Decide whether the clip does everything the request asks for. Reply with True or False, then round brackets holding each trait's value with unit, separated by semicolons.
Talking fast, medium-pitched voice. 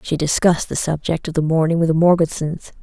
True (215 wpm; 160 Hz)